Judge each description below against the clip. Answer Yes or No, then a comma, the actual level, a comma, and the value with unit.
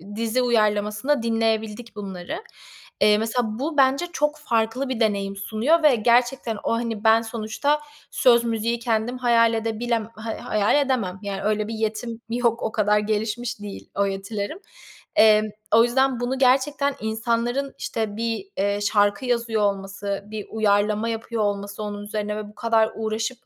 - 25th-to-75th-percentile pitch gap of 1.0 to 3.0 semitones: Yes, narrow, 2.4 semitones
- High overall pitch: Yes, high, 225 Hz